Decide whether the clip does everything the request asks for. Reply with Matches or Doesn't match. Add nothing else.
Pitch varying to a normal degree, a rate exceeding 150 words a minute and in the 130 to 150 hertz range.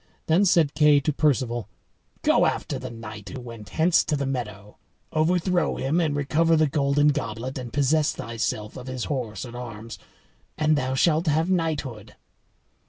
Matches